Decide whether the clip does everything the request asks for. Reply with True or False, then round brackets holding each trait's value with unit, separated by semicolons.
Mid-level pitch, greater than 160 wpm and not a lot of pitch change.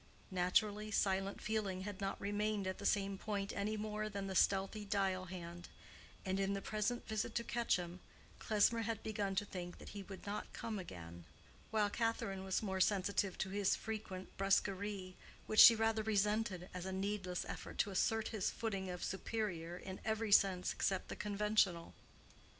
False (200 Hz; 170 wpm; 2.2 semitones)